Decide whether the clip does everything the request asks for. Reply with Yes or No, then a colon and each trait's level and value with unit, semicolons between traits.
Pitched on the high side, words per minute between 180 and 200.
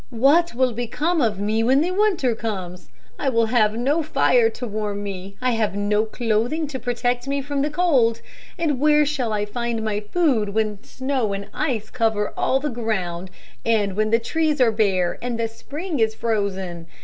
Yes: high, 230 Hz; average, 185 wpm